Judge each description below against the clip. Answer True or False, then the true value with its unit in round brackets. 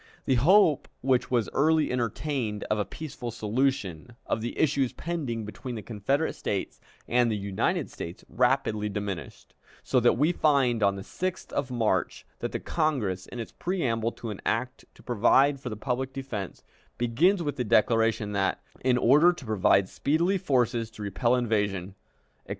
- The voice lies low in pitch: True (120 Hz)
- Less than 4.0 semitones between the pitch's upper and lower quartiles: False (4.4 semitones)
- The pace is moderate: True (165 wpm)